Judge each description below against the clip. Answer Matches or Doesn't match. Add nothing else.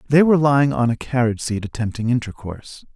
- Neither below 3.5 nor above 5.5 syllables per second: Doesn't match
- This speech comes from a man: Matches